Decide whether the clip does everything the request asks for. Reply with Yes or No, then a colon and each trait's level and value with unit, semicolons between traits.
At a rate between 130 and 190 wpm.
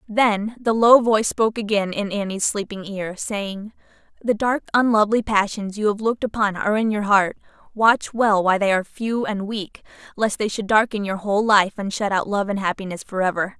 No: fast, 205 wpm